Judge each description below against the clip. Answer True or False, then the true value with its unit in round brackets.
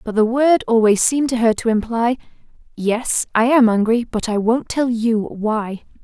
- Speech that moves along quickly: False (190 wpm)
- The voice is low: False (230 Hz)